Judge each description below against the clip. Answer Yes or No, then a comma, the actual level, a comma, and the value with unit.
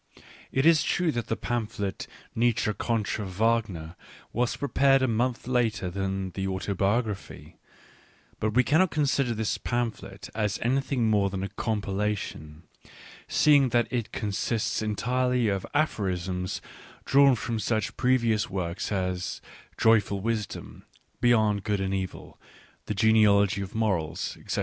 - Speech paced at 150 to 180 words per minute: No, slow, 135 wpm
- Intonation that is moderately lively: Yes, average, 3.8 semitones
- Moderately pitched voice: No, low, 110 Hz